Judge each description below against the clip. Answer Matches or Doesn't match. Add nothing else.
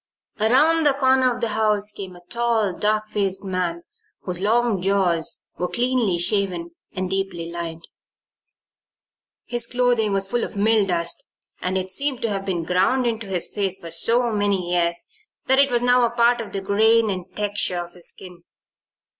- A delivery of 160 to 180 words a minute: Matches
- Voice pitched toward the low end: Doesn't match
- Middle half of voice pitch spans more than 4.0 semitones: Matches